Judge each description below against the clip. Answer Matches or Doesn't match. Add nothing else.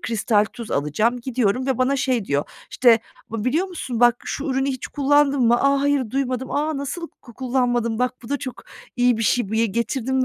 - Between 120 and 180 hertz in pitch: Doesn't match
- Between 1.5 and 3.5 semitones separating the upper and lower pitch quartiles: Matches